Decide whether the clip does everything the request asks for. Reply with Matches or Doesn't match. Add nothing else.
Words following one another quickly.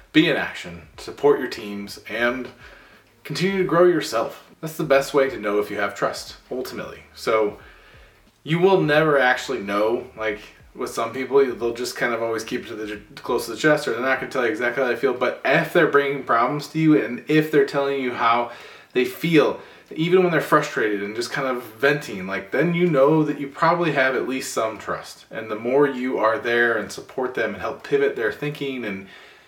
Matches